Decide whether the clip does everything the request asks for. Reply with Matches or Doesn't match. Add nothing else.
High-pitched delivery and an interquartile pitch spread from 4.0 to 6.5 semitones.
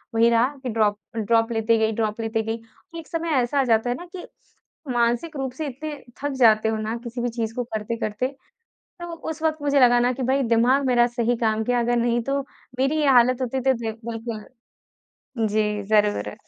Doesn't match